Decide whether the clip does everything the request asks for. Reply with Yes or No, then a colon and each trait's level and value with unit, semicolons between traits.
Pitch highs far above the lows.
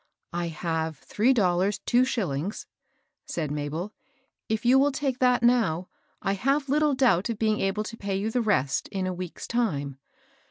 Yes: wide, 6.0 semitones